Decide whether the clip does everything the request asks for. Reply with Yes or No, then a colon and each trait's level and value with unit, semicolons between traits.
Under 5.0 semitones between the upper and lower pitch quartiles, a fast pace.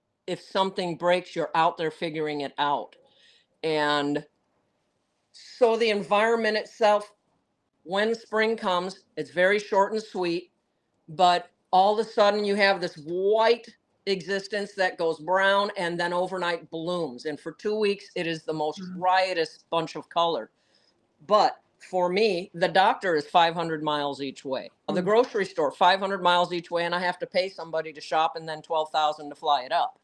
No: average, 3.8 semitones; average, 165 wpm